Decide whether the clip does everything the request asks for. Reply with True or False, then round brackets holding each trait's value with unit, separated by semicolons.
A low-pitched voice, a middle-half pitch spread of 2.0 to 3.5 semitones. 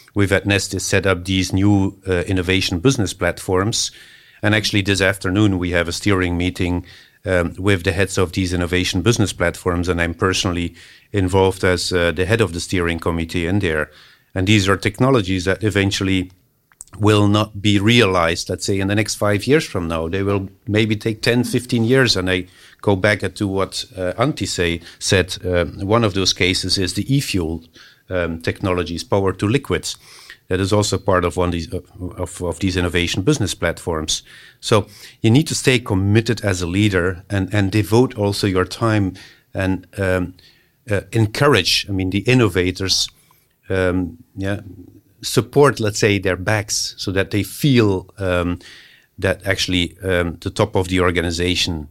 True (95 Hz; 2.6 semitones)